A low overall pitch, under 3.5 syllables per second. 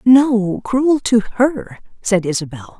No: high, 220 Hz; 3.3 syllables/s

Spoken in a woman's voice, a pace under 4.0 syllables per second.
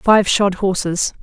Yes: female; 3.5 syllables/s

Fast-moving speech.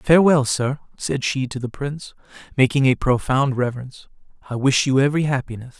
No: average, 165 wpm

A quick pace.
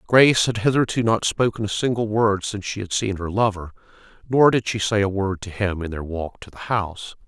Yes: fast, 230 wpm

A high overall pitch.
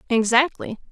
Yes: high, 240 Hz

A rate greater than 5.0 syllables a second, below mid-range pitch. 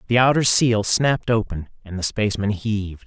Yes: 5.5 syllables/s; low, 110 Hz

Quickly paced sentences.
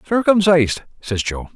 No: slow, 115 wpm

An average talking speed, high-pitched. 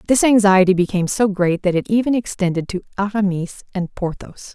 Yes: average, 170 wpm; high, 195 Hz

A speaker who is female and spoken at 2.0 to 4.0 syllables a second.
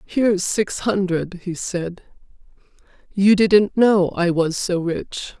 Yes: female; 3.4 syllables/s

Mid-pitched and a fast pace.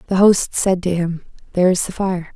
Yes: medium, 180 Hz; fast, 230 wpm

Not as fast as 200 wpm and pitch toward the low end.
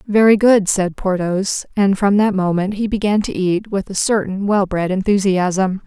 No: average, 185 wpm; high, 195 Hz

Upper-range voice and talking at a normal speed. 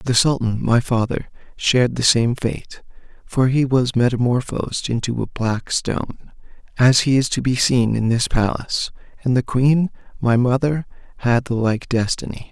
No: low, 125 Hz; average, 165 wpm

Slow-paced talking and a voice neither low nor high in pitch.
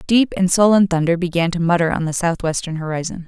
No: average, 200 wpm; medium, 175 Hz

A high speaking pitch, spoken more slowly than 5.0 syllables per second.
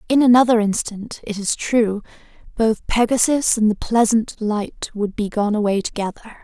Yes: high, 220 Hz; 4.7 syllables/s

